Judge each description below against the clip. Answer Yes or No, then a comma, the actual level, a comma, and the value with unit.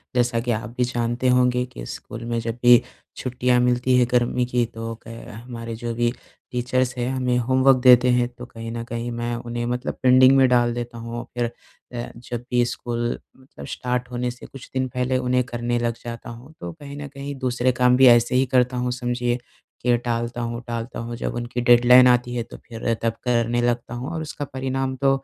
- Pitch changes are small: Yes, narrow, 1.1 semitones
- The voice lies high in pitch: No, low, 120 Hz